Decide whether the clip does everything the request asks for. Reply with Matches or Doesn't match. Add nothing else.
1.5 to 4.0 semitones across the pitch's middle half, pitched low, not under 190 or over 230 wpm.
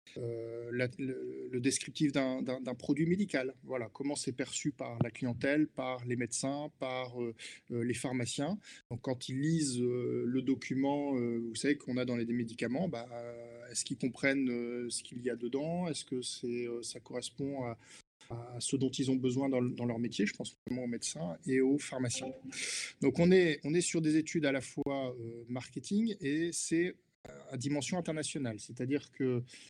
Matches